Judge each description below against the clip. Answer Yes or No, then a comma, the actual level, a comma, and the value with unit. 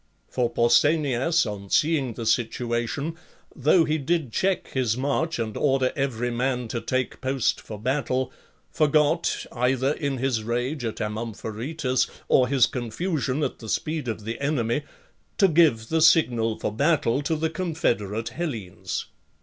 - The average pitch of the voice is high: No, low, 130 Hz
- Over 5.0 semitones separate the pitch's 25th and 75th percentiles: No, average, 4.7 semitones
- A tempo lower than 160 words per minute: Yes, average, 150 wpm